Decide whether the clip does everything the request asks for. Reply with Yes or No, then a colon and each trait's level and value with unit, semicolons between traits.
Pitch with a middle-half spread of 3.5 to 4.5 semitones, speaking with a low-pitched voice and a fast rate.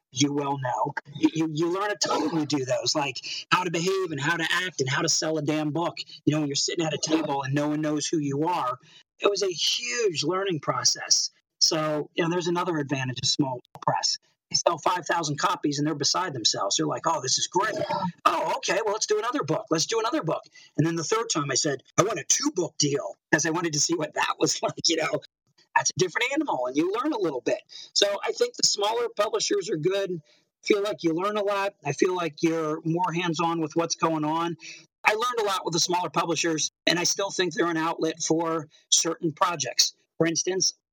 No: average, 3.8 semitones; medium, 165 Hz; fast, 240 wpm